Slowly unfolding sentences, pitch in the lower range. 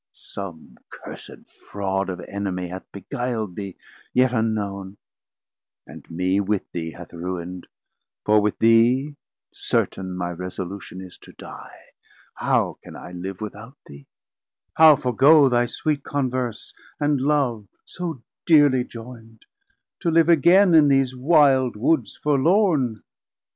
Yes: slow, 125 wpm; low, 115 Hz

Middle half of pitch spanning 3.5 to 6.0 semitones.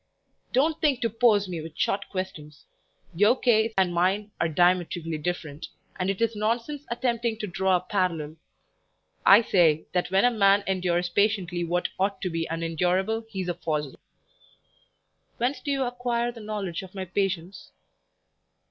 Yes: average, 4.2 semitones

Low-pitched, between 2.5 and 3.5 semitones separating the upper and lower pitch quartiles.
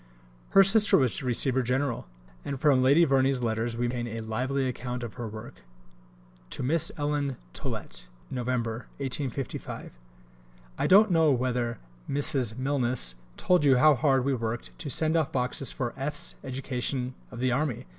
Yes: low, 130 Hz; average, 2.9 semitones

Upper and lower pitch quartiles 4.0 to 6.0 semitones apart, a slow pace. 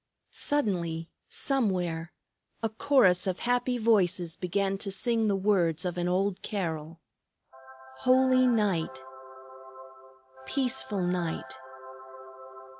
Yes: average, 4.9 semitones; slow, 95 wpm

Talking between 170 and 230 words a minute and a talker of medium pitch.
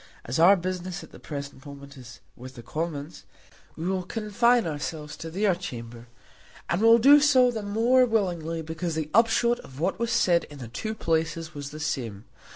Yes: average, 185 wpm; medium, 165 Hz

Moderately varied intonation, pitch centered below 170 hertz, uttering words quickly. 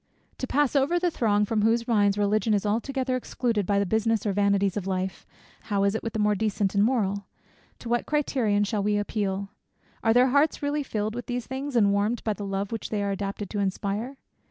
No: average, 3.3 semitones; high, 210 Hz; fast, 225 wpm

